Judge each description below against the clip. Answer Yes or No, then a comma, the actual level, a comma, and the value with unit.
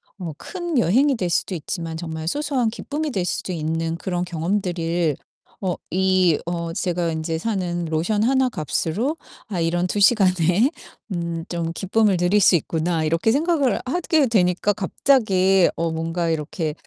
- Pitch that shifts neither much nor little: Yes, average, 4.7 semitones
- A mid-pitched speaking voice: Yes, medium, 180 Hz